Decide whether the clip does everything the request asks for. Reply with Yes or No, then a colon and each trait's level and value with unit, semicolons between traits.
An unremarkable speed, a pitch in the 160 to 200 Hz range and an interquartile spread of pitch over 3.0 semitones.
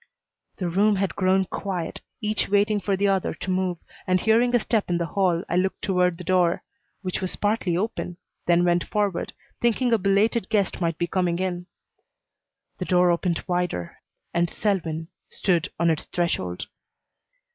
No: average, 170 wpm; medium, 185 Hz; narrow, 2.6 semitones